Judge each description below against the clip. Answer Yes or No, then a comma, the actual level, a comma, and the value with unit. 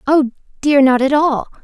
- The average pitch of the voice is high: Yes, very high, 275 Hz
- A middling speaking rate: Yes, average, 185 wpm